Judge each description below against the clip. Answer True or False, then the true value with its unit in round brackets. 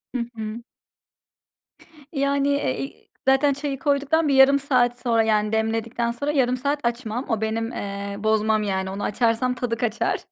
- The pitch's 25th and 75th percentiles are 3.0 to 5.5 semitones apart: True (3.8 semitones)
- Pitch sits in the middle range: False (235 Hz)